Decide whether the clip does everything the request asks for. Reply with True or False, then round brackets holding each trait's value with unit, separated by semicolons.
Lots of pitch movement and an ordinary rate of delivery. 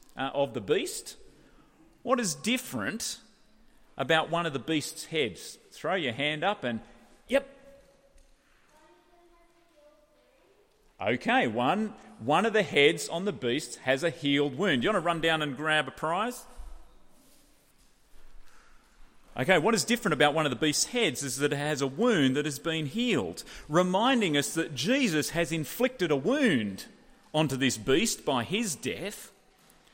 True (8.9 semitones; 150 wpm)